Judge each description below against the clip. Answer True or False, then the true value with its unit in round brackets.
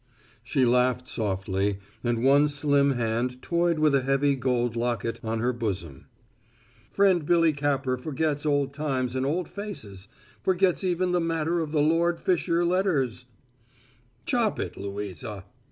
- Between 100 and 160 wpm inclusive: True (145 wpm)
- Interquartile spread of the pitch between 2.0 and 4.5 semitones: False (5.6 semitones)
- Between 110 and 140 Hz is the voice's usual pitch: True (135 Hz)